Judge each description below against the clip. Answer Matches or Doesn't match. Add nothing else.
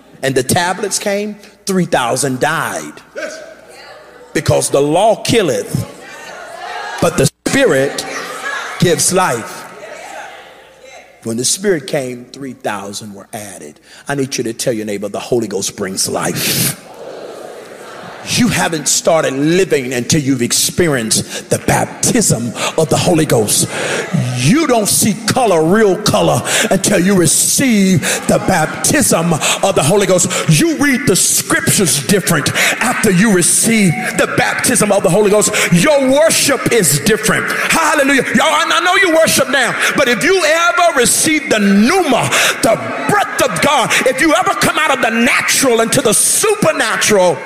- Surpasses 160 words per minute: Doesn't match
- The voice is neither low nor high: Doesn't match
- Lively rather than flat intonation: Matches